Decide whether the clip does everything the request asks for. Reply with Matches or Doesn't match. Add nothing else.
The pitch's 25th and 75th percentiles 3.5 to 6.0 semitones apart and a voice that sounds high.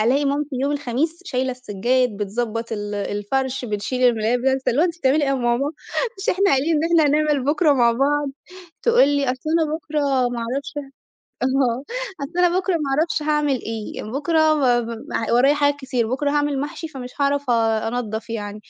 Matches